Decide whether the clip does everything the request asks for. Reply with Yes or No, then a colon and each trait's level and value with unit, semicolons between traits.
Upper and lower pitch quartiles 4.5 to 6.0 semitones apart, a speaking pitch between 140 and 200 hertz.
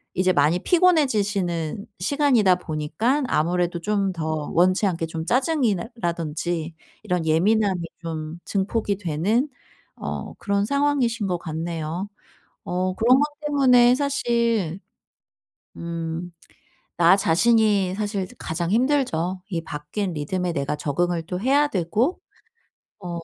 Yes: wide, 5.4 semitones; medium, 185 Hz